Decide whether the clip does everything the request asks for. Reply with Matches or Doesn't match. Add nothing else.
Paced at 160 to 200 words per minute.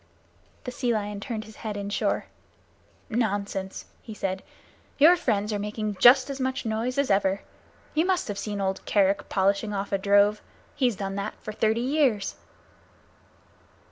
Doesn't match